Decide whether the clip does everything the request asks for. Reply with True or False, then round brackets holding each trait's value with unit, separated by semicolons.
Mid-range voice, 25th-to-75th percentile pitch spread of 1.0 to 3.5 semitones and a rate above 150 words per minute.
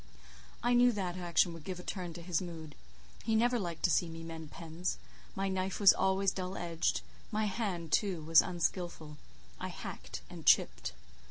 True (180 Hz; 2.8 semitones; 175 wpm)